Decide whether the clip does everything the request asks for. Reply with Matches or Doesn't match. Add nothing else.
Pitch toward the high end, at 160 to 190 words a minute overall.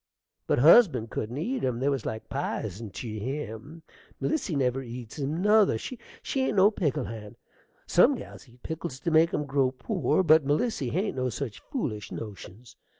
Doesn't match